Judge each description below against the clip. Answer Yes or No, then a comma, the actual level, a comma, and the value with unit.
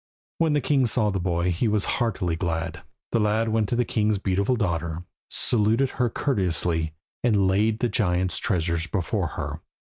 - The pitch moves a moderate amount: Yes, average, 4.6 semitones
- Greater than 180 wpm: No, average, 170 wpm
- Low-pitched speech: Yes, low, 105 Hz